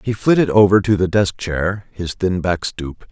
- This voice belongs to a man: Yes, male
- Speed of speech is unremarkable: No, fast, 210 wpm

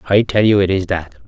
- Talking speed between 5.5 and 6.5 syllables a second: Yes, 5.6 syllables/s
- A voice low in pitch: Yes, very low, 95 Hz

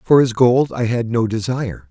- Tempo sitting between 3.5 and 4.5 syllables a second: No, 5.0 syllables/s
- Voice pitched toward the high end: No, low, 115 Hz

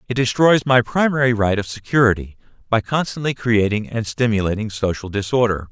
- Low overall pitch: Yes, low, 115 Hz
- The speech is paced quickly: No, average, 145 wpm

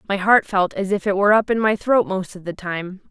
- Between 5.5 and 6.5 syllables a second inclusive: Yes, 5.6 syllables/s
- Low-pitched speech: No, high, 195 Hz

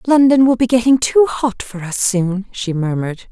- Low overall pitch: No, high, 225 Hz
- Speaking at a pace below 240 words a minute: Yes, average, 200 wpm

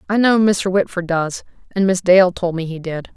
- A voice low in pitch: No, medium, 185 Hz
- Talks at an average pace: No, fast, 230 wpm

